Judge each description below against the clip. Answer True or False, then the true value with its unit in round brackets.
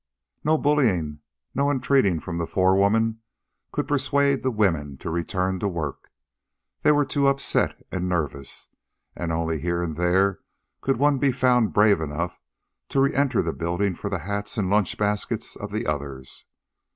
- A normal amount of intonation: False (7.5 semitones)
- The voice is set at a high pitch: False (100 Hz)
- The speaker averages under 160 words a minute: False (165 wpm)